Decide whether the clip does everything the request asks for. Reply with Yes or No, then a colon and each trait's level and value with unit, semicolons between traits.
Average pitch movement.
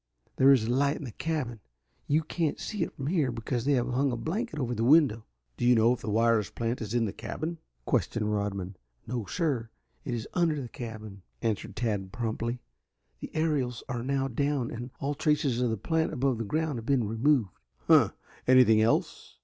Yes: average, 4.1 semitones